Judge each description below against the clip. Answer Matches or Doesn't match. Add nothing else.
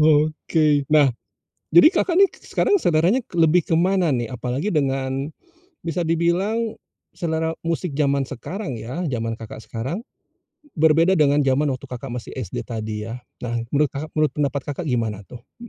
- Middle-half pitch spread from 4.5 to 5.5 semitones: Matches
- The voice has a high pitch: Doesn't match